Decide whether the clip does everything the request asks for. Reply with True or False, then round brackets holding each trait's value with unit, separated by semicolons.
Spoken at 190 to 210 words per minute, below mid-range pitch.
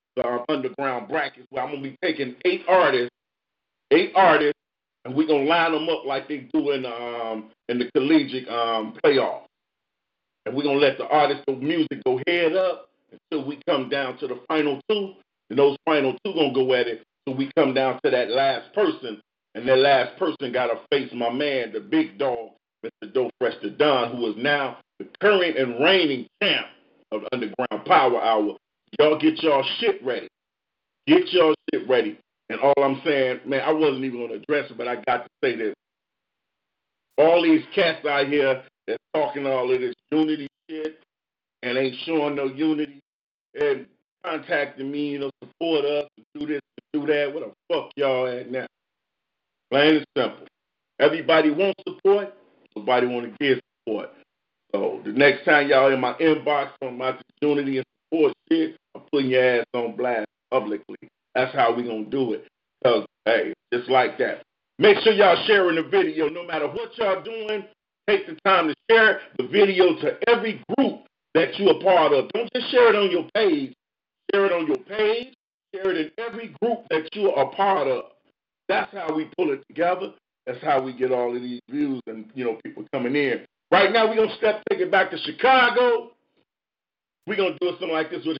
False (195 wpm; 155 Hz)